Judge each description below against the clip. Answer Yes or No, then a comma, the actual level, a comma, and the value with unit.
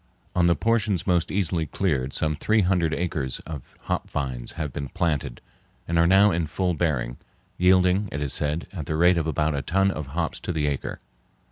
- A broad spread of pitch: No, average, 3.8 semitones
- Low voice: Yes, very low, 85 Hz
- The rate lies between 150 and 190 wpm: No, average, 200 wpm